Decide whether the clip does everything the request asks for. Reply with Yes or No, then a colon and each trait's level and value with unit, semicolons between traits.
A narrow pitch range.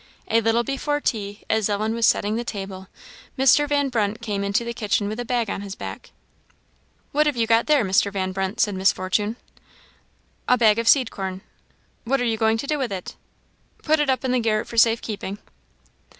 No: average, 3.5 semitones